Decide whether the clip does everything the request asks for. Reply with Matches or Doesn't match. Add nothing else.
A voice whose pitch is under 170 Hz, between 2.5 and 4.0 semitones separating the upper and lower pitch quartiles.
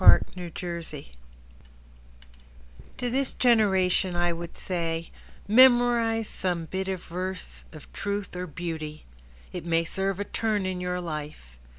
Doesn't match